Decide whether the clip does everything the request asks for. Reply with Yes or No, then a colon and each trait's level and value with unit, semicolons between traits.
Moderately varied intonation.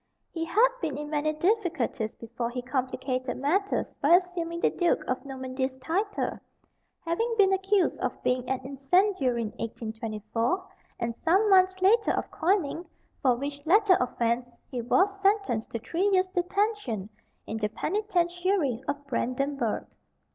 No: wide, 7.1 semitones